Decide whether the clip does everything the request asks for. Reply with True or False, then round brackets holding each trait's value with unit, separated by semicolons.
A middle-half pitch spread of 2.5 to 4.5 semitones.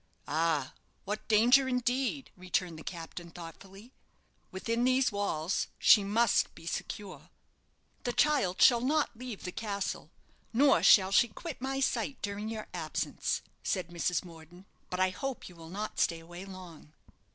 False (5.5 semitones)